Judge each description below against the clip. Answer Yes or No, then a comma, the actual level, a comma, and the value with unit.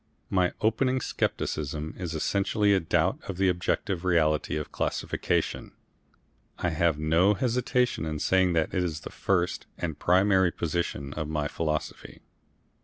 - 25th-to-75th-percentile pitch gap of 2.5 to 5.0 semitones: Yes, average, 3.8 semitones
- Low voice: Yes, very low, 90 Hz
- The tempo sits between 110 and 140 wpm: Yes, slow, 135 wpm